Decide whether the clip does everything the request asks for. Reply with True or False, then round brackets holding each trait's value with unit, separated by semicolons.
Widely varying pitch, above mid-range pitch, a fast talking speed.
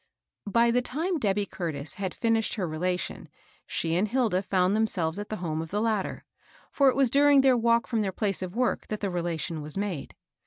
False (4.7 semitones; 205 Hz; 210 wpm)